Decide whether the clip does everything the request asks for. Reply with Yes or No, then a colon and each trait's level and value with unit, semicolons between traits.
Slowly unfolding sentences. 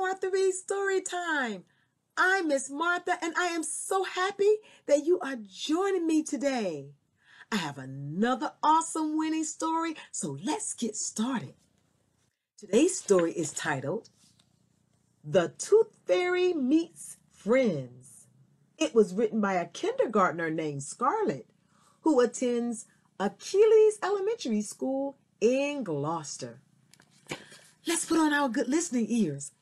Yes: slow, 115 wpm